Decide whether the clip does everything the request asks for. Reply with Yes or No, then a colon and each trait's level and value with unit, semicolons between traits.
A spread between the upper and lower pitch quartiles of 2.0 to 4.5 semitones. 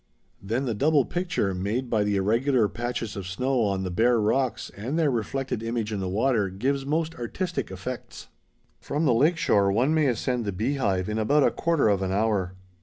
No: average, 5.1 semitones